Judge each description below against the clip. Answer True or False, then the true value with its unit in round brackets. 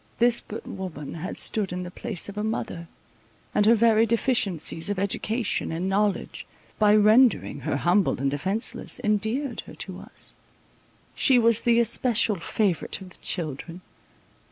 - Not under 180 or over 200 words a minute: False (150 wpm)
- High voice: True (205 Hz)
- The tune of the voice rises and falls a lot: False (4.3 semitones)